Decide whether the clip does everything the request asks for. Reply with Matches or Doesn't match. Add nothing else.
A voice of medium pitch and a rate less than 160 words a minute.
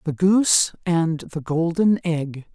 Matches